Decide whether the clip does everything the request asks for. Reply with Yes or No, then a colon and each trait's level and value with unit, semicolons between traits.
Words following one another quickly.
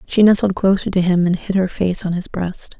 Yes: fast, 255 wpm